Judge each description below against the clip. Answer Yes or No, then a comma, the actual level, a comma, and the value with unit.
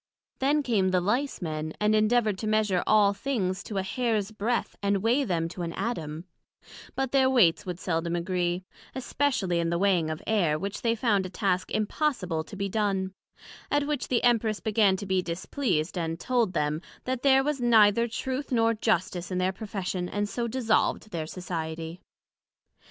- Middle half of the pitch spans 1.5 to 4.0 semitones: No, average, 4.7 semitones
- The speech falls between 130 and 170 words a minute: No, average, 180 wpm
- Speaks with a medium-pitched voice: No, high, 200 Hz